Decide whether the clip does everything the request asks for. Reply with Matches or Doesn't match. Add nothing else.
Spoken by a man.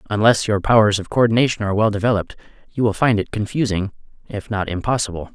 Matches